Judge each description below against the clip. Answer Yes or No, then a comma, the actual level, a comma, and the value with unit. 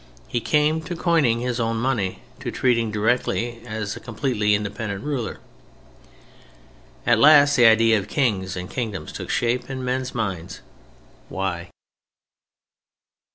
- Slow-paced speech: Yes, slow, 130 wpm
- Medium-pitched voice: No, low, 115 Hz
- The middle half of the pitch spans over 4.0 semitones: No, average, 3.5 semitones